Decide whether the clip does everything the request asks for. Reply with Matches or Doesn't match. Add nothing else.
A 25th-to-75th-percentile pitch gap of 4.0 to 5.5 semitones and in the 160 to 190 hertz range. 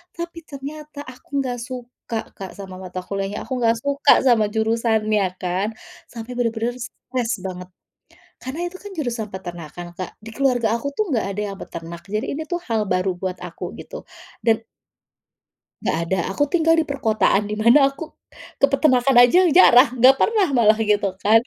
Doesn't match